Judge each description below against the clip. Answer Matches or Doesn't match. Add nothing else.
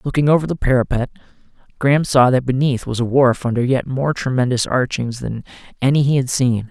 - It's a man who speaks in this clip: Matches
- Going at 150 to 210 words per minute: Matches